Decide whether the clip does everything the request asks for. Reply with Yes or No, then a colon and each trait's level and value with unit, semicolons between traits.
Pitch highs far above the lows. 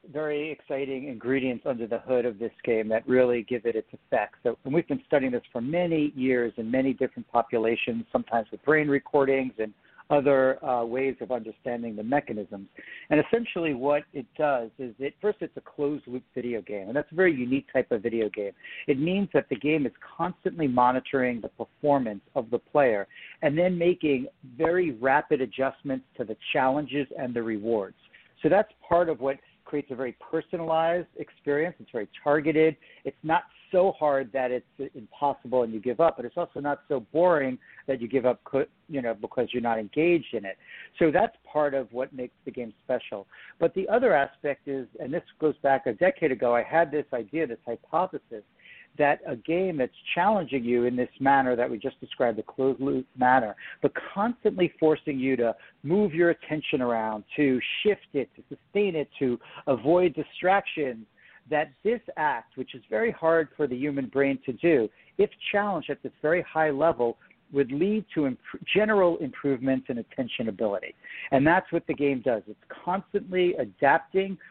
No: average, 4.6 semitones